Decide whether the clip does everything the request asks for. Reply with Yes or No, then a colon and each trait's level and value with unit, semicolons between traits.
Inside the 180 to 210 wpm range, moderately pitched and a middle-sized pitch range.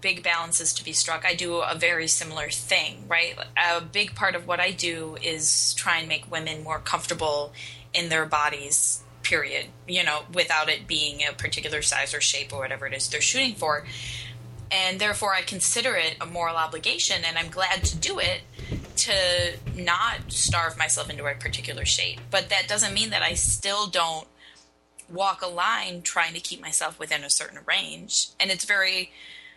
Yes: average, 185 wpm; medium, 160 Hz; average, 4.0 semitones